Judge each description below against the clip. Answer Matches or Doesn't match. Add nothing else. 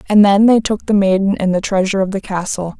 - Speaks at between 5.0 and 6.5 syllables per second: Matches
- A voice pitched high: Matches